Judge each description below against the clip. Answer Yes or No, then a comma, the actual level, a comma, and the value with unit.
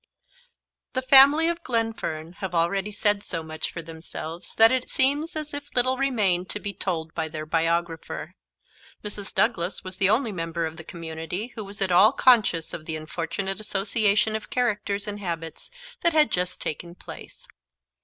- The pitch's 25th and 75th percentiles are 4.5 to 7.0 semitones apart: Yes, wide, 5.4 semitones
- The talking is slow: No, average, 170 wpm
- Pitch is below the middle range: No, high, 195 Hz